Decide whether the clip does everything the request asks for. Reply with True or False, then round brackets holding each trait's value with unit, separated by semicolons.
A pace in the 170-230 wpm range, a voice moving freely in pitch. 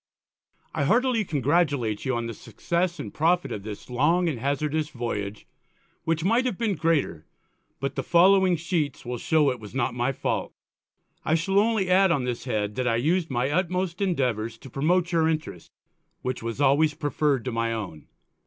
True (180 wpm; 6.3 semitones)